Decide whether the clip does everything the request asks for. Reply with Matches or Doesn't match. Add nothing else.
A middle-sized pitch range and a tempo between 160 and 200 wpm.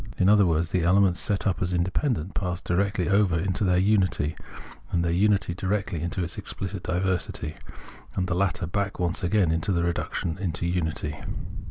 Doesn't match